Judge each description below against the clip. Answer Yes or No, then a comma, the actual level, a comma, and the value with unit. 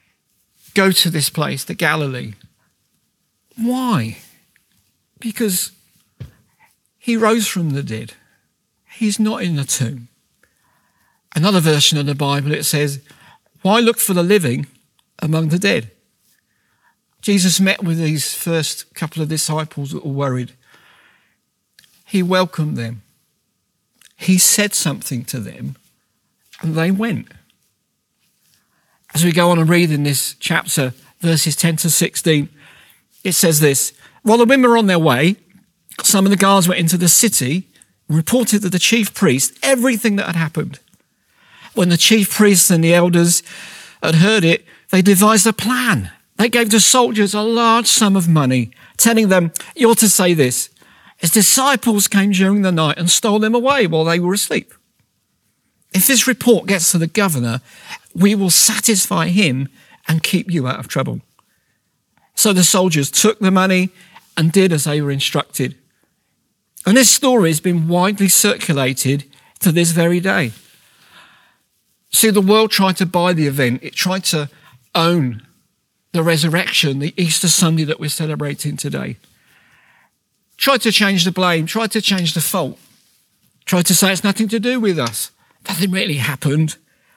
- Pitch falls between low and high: Yes, medium, 175 Hz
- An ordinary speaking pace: Yes, average, 155 wpm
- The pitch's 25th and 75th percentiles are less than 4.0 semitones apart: No, average, 4.8 semitones